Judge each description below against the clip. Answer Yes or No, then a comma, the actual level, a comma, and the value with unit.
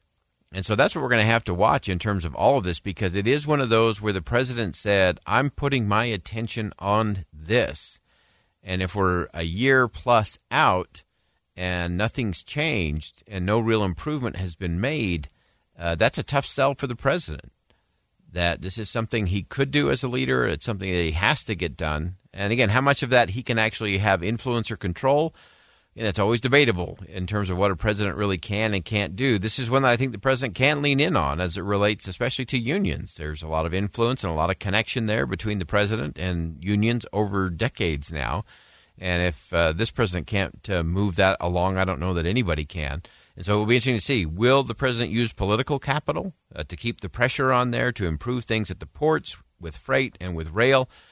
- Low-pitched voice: Yes, low, 105 Hz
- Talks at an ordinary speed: No, fast, 220 wpm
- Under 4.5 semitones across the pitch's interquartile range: No, average, 5.1 semitones